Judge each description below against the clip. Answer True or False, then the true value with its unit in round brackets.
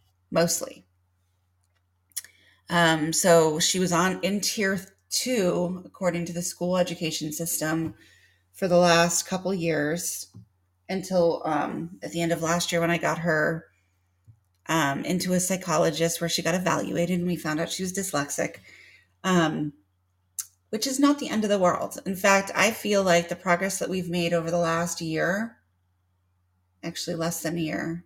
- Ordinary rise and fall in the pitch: False (7.6 semitones)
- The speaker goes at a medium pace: True (160 wpm)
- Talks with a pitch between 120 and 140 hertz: False (170 Hz)